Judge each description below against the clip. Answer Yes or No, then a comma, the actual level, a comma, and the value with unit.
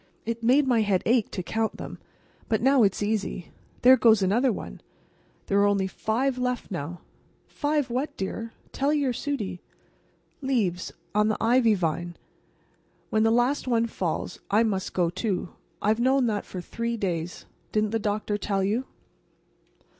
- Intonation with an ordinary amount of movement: Yes, average, 4.0 semitones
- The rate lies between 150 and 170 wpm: Yes, average, 160 wpm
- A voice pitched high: Yes, high, 220 Hz